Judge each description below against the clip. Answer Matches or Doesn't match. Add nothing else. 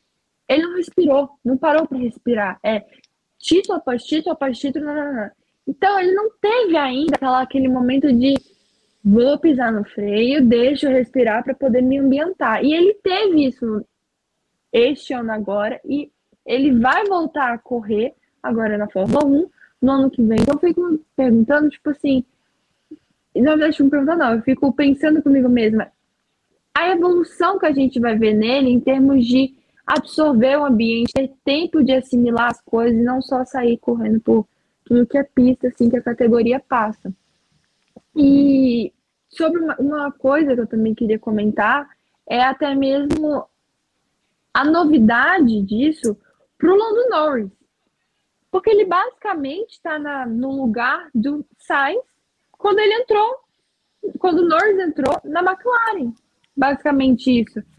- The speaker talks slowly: Doesn't match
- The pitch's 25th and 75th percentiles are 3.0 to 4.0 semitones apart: Doesn't match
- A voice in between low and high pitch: Doesn't match